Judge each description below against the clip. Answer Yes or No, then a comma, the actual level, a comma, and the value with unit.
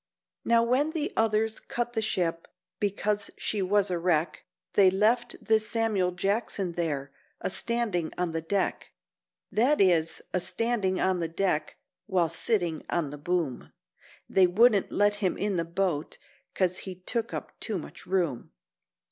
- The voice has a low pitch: No, high, 190 Hz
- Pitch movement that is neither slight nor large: Yes, average, 4.0 semitones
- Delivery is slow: No, average, 155 wpm